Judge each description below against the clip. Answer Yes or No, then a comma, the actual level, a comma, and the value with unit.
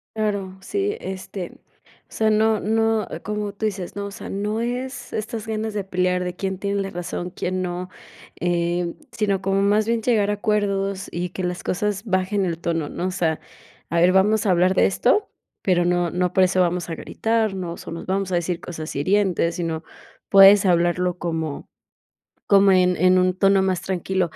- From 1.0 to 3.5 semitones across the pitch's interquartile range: Yes, narrow, 2.6 semitones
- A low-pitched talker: No, high, 190 Hz